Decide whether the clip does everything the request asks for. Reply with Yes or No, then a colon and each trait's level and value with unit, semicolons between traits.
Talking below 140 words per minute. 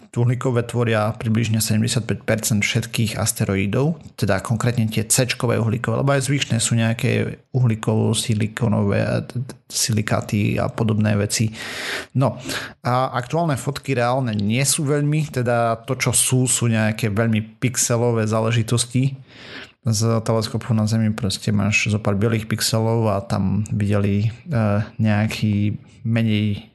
Yes: average, 125 wpm